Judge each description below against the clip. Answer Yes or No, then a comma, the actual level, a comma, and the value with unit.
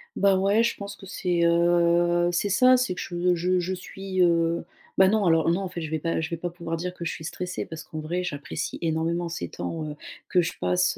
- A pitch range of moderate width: No, narrow, 1.8 semitones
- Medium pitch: Yes, medium, 175 Hz